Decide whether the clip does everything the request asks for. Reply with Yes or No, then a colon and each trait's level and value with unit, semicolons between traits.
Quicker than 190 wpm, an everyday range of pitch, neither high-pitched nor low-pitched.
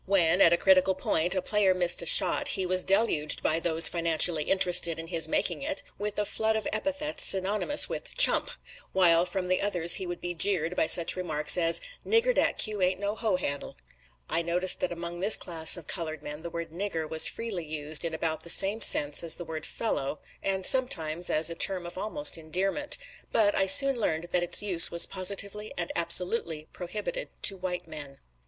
Yes: average, 200 wpm; average, 3.4 semitones; medium, 180 Hz